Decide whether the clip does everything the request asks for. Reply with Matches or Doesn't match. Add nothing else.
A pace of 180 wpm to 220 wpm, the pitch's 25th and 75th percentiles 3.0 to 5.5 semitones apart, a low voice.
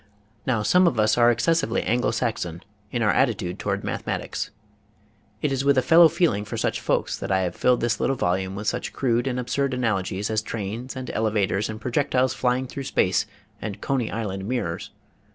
Matches